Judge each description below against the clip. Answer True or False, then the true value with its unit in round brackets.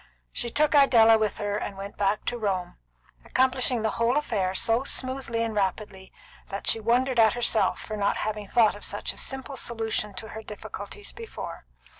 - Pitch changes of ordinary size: True (3.1 semitones)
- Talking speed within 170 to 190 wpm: True (180 wpm)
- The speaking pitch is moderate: False (225 Hz)